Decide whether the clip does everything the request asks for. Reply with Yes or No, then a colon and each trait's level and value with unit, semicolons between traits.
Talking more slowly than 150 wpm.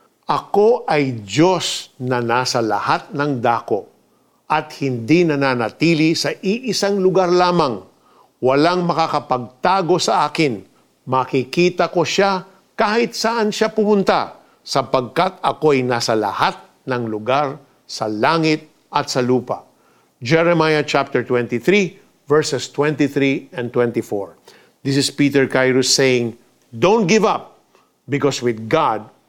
Yes: average, 115 wpm